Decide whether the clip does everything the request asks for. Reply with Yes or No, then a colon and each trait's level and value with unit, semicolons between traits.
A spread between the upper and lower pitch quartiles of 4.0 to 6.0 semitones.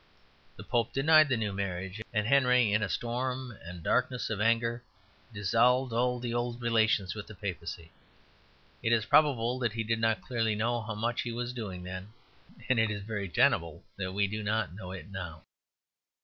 No: average, 3.3 semitones